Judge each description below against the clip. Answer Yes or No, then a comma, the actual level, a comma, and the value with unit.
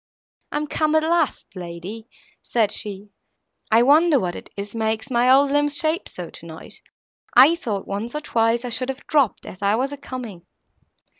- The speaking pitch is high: Yes, high, 245 Hz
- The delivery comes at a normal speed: Yes, average, 180 wpm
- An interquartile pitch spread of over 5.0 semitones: Yes, wide, 5.6 semitones